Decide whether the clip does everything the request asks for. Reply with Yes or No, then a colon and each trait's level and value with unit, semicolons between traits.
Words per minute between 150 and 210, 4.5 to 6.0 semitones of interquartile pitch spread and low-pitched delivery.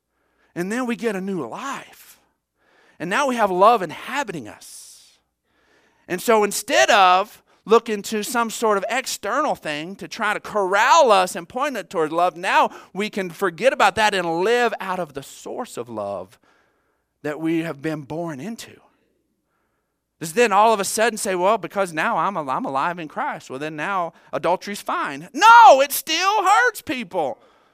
No: average, 170 wpm; average, 5.2 semitones; high, 205 Hz